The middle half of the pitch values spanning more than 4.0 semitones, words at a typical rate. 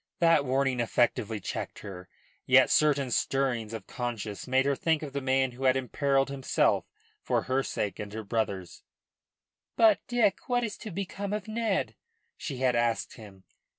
Yes: average, 5.2 semitones; average, 165 wpm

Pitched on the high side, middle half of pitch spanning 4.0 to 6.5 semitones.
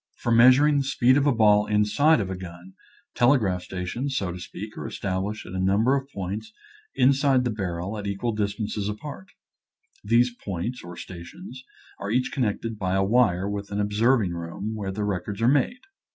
No: low, 105 Hz; average, 4.6 semitones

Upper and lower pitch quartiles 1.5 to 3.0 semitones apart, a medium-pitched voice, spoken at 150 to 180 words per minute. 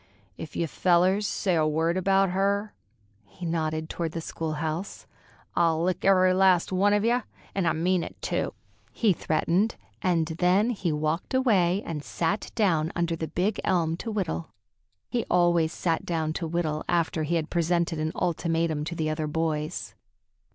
Yes: average, 2.7 semitones; medium, 170 Hz; average, 165 wpm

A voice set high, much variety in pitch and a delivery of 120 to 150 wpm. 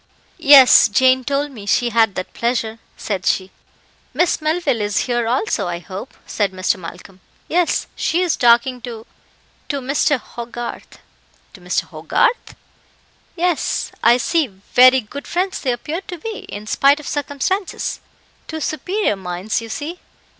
Yes: very high, 250 Hz; wide, 6.0 semitones; average, 145 wpm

